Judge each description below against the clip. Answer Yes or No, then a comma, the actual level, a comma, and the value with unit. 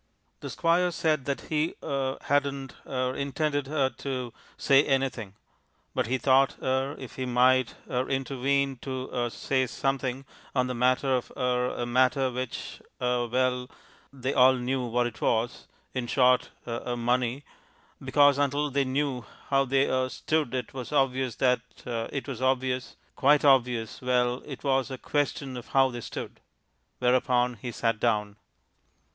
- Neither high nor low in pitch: No, low, 130 Hz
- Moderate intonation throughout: No, narrow, 1.7 semitones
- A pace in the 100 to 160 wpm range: Yes, average, 155 wpm